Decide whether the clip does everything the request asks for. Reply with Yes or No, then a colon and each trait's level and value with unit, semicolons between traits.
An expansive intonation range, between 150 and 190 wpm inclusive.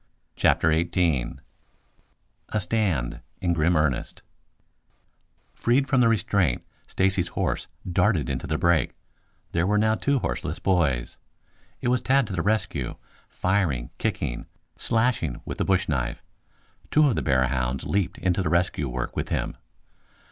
No: wide, 6.4 semitones; average, 140 wpm